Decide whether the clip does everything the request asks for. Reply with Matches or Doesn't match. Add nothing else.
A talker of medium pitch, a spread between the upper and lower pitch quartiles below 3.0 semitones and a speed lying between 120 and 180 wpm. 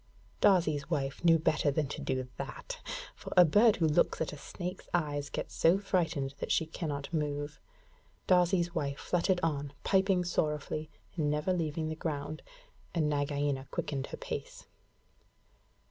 Doesn't match